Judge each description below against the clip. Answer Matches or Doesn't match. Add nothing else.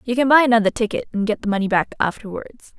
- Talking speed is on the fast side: Matches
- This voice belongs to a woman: Matches